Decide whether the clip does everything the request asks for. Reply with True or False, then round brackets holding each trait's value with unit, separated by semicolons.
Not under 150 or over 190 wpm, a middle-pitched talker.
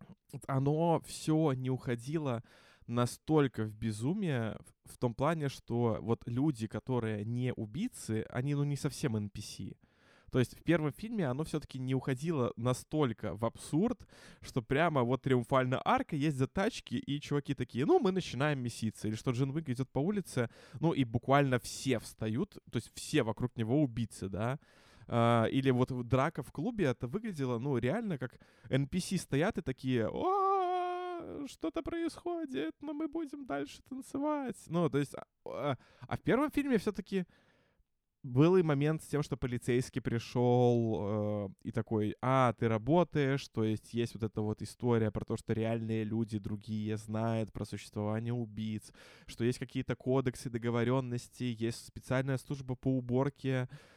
False (155 wpm; 130 Hz)